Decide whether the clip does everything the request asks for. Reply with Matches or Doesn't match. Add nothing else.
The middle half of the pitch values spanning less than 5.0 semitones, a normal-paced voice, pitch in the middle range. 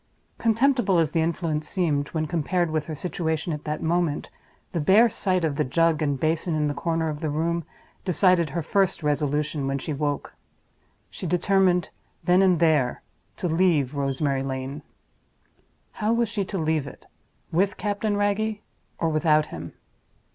Matches